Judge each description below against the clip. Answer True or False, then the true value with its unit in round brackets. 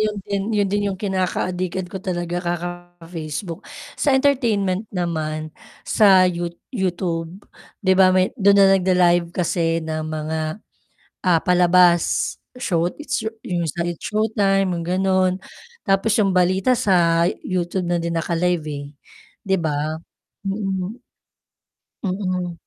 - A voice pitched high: False (180 Hz)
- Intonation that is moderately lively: False (2.3 semitones)